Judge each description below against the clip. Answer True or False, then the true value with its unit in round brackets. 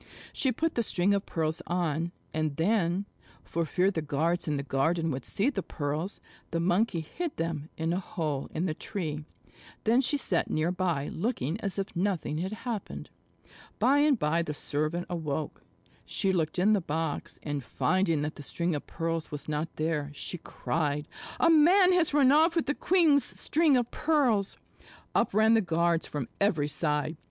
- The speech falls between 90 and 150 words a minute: False (180 wpm)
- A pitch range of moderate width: False (5.8 semitones)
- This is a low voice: False (170 Hz)